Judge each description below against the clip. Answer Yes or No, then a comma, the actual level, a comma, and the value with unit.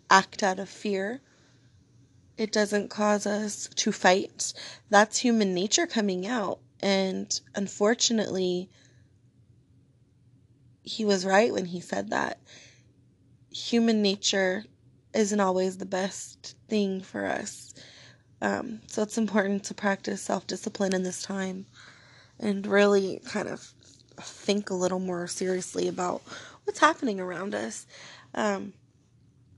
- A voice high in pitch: Yes, high, 195 Hz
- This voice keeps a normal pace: No, slow, 120 wpm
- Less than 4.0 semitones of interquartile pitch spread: Yes, average, 2.8 semitones